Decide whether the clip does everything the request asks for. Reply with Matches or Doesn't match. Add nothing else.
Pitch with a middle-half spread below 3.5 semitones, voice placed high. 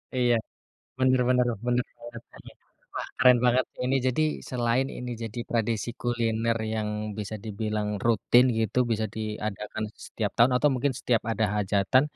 Doesn't match